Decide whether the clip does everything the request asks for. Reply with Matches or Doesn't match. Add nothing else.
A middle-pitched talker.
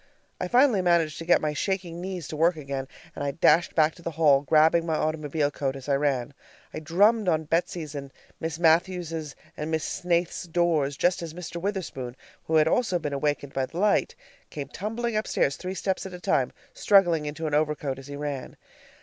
Matches